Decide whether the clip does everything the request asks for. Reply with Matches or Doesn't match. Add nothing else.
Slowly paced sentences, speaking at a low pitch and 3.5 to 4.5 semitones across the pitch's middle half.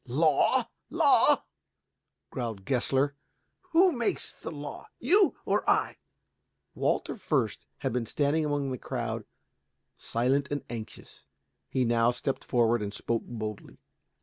Matches